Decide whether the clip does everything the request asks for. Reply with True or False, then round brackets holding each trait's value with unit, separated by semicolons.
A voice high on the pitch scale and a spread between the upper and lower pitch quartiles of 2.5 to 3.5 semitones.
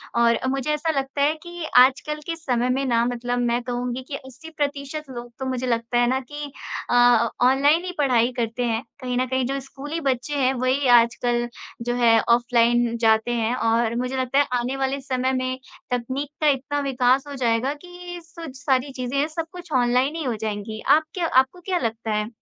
True (255 Hz; 2.8 semitones)